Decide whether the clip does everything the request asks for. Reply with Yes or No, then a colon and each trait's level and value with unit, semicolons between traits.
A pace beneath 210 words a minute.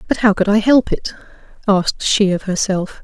Yes: average, 200 wpm